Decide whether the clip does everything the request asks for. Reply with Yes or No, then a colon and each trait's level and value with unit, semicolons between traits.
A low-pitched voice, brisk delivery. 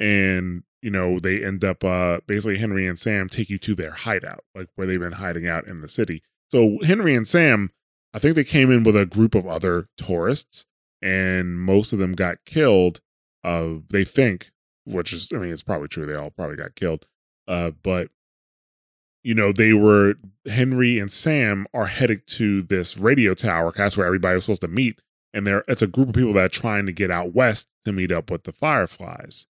Yes: low, 100 Hz; fast, 210 wpm